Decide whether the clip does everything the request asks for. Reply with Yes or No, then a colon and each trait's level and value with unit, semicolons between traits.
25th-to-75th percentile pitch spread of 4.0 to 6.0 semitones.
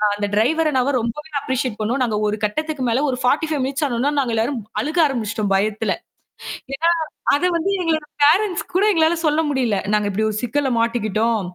Yes: wide, 5.5 semitones